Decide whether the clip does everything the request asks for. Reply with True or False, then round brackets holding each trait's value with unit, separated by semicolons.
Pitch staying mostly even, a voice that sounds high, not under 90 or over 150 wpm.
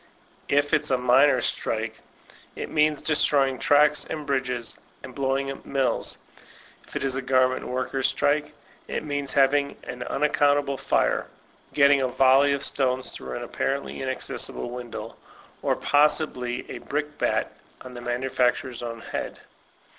False (2.2 semitones; 135 Hz; 145 wpm)